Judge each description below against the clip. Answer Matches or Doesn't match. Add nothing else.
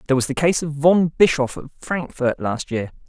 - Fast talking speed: Matches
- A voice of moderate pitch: Matches